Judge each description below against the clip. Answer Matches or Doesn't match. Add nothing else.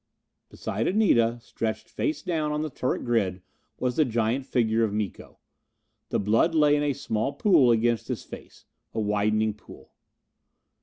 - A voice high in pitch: Doesn't match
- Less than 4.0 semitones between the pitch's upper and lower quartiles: Doesn't match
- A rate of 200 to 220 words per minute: Doesn't match